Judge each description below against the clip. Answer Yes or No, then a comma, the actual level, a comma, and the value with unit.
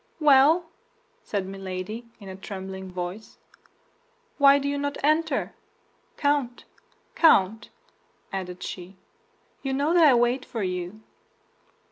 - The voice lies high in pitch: Yes, high, 225 Hz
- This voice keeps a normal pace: No, slow, 115 wpm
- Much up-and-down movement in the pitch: Yes, wide, 7.0 semitones